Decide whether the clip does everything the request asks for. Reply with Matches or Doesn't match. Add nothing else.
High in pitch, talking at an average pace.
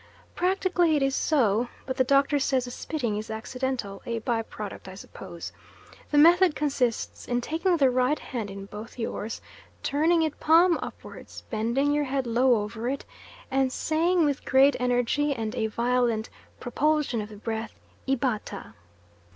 Matches